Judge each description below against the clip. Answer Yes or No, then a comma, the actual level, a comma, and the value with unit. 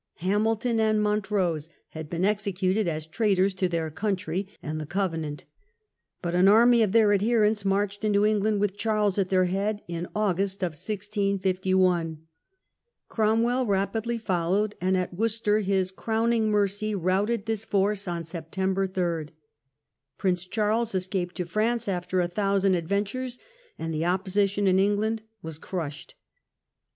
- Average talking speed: Yes, average, 150 wpm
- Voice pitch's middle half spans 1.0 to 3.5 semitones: Yes, average, 2.8 semitones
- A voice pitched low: No, high, 195 Hz